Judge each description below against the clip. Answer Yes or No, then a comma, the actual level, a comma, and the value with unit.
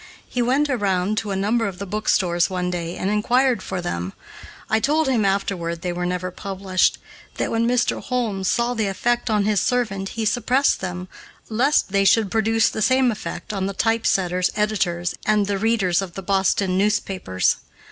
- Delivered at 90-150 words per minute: No, average, 180 wpm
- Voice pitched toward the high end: Yes, high, 200 Hz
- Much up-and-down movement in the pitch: No, average, 3.6 semitones